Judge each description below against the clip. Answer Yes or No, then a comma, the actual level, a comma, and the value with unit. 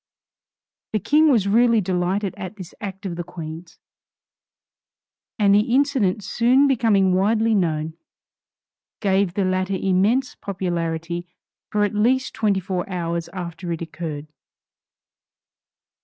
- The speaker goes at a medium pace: No, slow, 120 wpm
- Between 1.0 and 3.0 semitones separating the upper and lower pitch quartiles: No, average, 3.6 semitones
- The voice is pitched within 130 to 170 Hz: No, high, 195 Hz